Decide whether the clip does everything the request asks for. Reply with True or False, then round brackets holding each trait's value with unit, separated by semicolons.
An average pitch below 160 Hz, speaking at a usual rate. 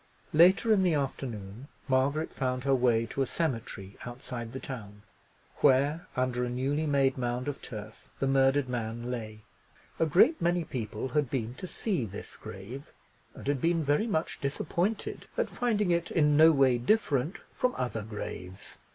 True (135 Hz; 165 wpm)